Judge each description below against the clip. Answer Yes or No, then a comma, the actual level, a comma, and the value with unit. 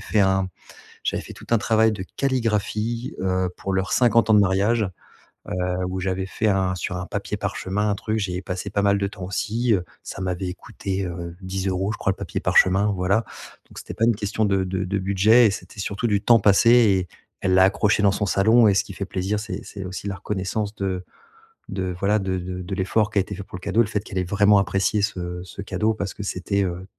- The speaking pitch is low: Yes, low, 100 Hz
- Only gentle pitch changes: Yes, narrow, 2.2 semitones